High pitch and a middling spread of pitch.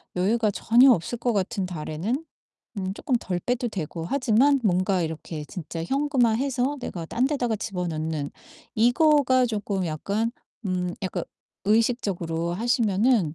No: high, 210 Hz; wide, 5.8 semitones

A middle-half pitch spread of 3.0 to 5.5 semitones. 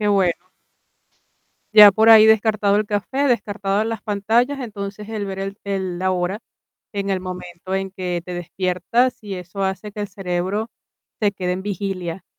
No: narrow, 2.4 semitones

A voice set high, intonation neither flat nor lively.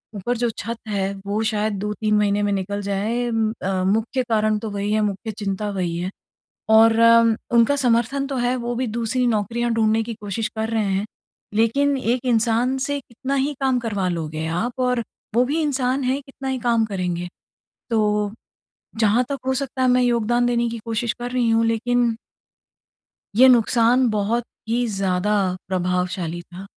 Yes: high, 225 Hz; average, 3.0 semitones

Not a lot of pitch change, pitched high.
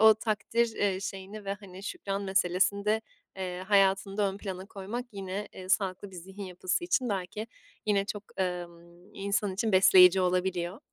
Yes: narrow, 1.9 semitones; high, 195 Hz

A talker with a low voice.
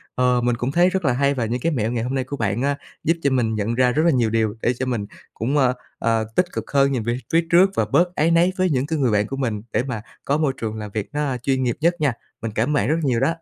Yes: low, 130 Hz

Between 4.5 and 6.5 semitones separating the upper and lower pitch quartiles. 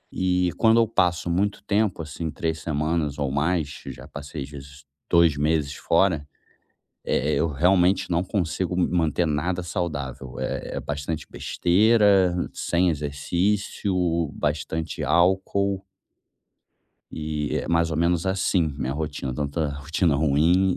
No: average, 3.7 semitones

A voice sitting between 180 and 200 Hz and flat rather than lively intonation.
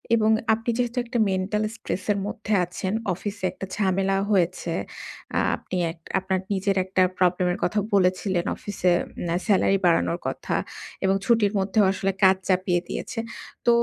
Yes: high, 190 Hz; narrow, 2.1 semitones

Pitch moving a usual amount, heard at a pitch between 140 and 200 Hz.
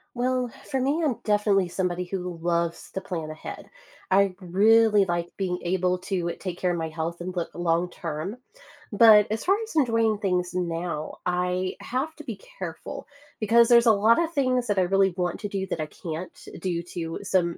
Yes: average, 4.0 semitones; medium, 185 Hz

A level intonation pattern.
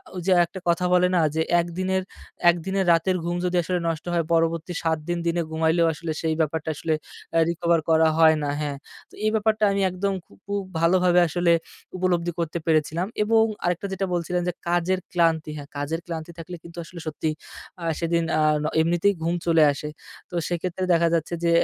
Yes: narrow, 1.9 semitones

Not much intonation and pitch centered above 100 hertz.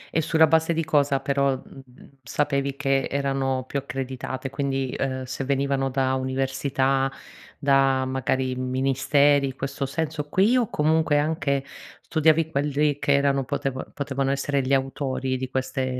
Yes: narrow, 1.5 semitones; low, 135 Hz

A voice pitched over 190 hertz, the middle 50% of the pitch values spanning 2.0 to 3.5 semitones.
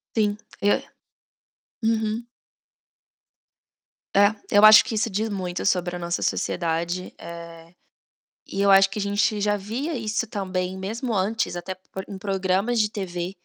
Yes: high, 200 Hz; average, 2.8 semitones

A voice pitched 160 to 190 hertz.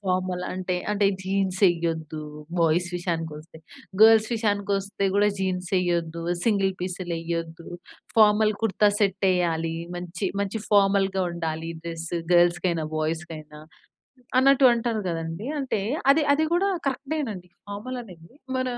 Yes: medium, 185 Hz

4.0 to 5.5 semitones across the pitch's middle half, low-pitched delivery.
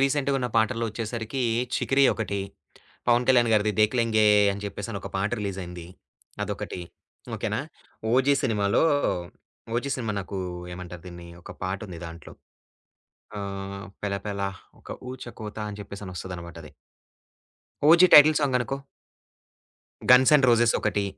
Yes: average, 4.3 semitones; low, 105 Hz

